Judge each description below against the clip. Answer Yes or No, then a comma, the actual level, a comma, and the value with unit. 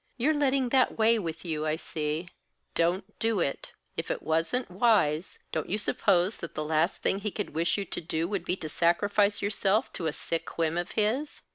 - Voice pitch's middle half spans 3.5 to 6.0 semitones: Yes, average, 4.8 semitones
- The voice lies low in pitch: No, medium, 185 Hz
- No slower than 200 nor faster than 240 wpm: Yes, fast, 205 wpm